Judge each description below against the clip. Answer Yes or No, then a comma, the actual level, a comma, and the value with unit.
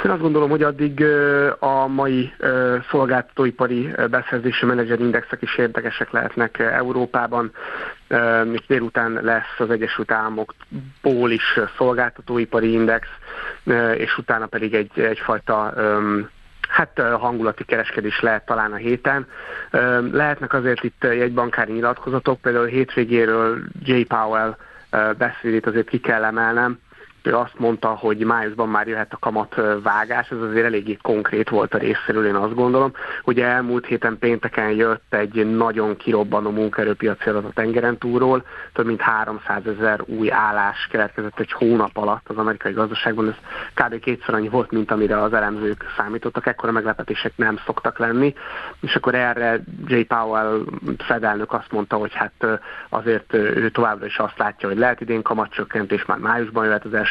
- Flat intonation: Yes, narrow, 2.1 semitones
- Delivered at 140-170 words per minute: Yes, average, 145 wpm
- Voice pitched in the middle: No, low, 115 Hz